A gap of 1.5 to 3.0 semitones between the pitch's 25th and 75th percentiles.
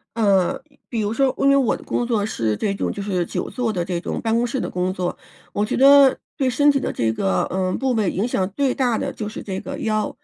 No: average, 5.2 semitones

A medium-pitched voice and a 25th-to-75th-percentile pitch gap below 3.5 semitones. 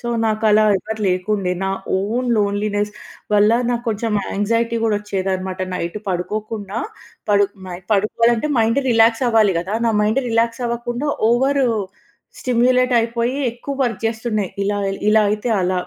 No: high, 220 Hz; narrow, 2.5 semitones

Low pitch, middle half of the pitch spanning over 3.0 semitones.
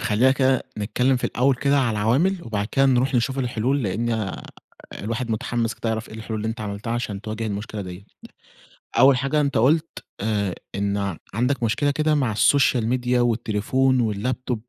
Yes: low, 120 Hz; average, 3.5 semitones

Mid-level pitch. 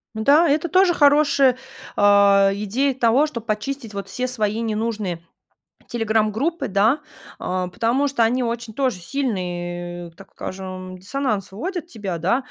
No: high, 225 Hz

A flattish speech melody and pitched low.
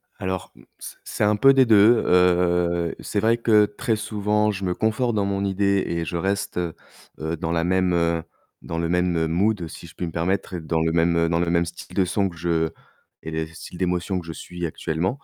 No: average, 3.3 semitones; very low, 90 Hz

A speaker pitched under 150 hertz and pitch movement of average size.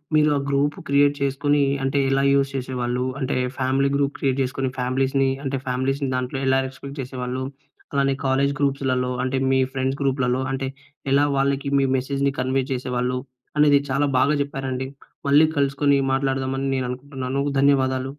No: low, 135 Hz; narrow, 1.2 semitones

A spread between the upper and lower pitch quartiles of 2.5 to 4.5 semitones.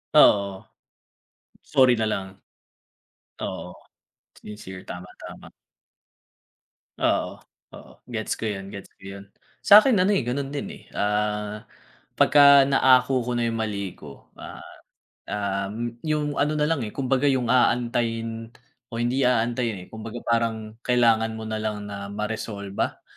Yes: average, 3.4 semitones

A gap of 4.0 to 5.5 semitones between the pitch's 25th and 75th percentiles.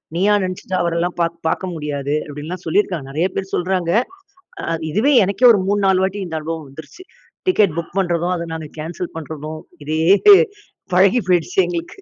No: average, 3.2 semitones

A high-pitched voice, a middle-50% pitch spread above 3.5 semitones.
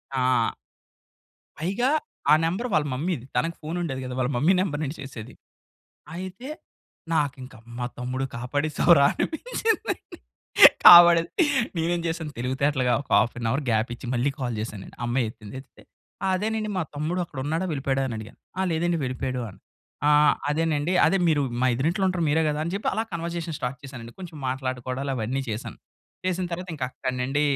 No: medium, 145 Hz; average, 5.0 semitones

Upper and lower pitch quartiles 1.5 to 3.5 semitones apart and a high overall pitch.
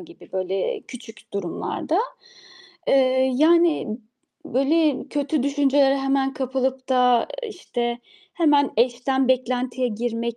Yes: average, 2.8 semitones; very high, 260 Hz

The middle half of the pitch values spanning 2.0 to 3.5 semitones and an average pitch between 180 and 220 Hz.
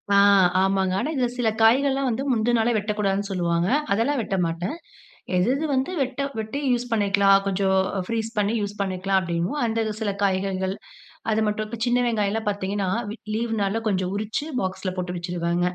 Yes: average, 3.2 semitones; high, 205 Hz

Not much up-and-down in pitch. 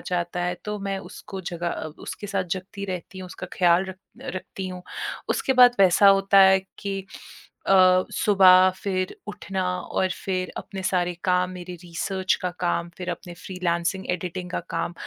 Yes: narrow, 1.4 semitones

